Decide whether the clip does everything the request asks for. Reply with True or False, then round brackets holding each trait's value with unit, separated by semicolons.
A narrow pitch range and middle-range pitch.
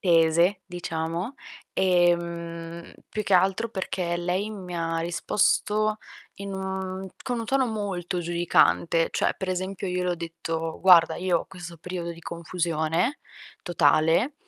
True (2.2 semitones; 175 Hz)